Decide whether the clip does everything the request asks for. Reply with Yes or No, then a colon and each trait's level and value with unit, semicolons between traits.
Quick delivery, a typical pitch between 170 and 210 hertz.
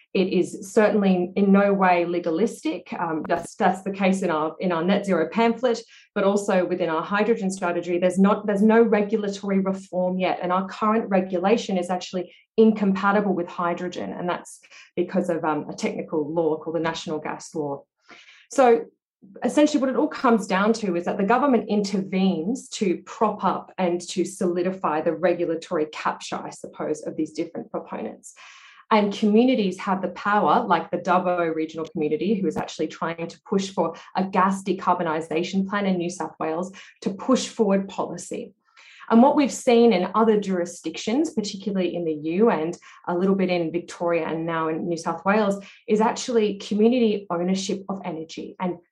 No: average, 175 wpm; medium, 185 Hz